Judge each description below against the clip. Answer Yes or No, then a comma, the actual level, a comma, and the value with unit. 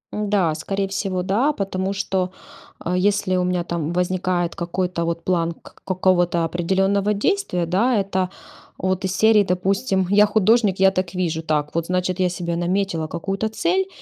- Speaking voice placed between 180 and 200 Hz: Yes, medium, 185 Hz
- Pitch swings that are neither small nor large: No, narrow, 2.2 semitones